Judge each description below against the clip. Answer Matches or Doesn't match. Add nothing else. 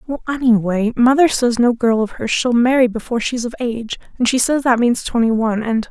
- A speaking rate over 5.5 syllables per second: Matches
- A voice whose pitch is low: Doesn't match